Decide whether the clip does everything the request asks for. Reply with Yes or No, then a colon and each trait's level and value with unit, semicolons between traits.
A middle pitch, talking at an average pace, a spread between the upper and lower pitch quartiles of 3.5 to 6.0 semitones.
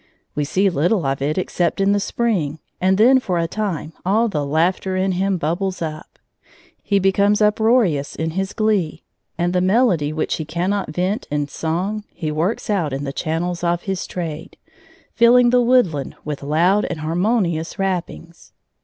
Yes: medium, 180 Hz; average, 170 wpm; average, 4.2 semitones